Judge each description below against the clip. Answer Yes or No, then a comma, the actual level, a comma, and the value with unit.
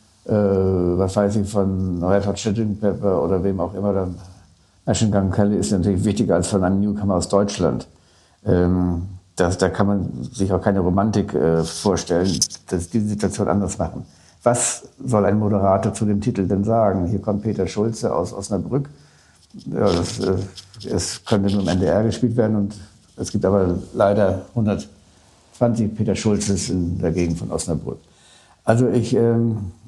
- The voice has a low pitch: Yes, low, 100 Hz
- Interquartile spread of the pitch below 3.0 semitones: Yes, narrow, 2.5 semitones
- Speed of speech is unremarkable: Yes, average, 160 wpm